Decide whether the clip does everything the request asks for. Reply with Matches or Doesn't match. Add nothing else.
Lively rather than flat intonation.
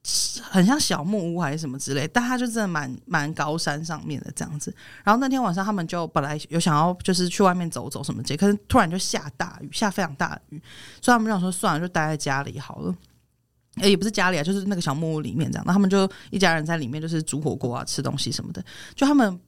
Doesn't match